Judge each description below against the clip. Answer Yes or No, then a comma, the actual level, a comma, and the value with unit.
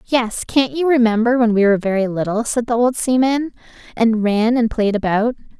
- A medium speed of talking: Yes, average, 195 wpm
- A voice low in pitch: No, high, 230 Hz